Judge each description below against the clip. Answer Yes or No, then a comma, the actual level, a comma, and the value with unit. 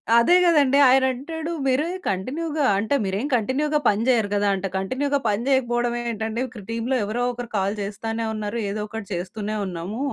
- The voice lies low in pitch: No, high, 230 Hz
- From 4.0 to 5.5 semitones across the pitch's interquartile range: Yes, average, 4.4 semitones